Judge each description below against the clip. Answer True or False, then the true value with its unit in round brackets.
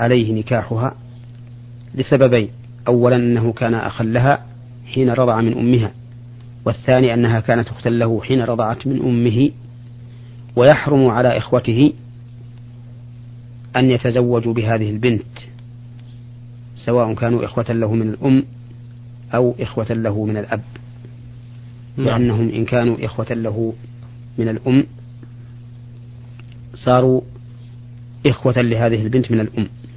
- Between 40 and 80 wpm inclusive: False (105 wpm)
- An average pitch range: False (0.6 semitones)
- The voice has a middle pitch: False (120 Hz)